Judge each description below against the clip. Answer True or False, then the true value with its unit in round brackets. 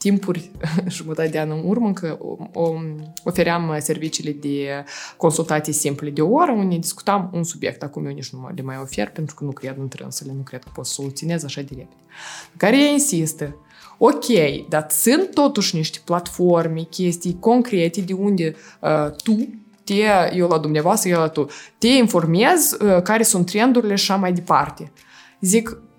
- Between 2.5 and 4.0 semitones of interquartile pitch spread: False (4.6 semitones)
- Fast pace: True (175 wpm)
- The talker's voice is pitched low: False (170 Hz)